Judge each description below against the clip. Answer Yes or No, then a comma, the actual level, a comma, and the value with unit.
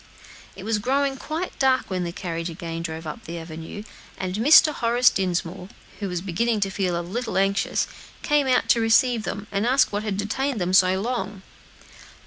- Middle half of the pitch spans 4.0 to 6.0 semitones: Yes, average, 5.2 semitones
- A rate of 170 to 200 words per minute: Yes, average, 185 wpm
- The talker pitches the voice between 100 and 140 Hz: No, high, 200 Hz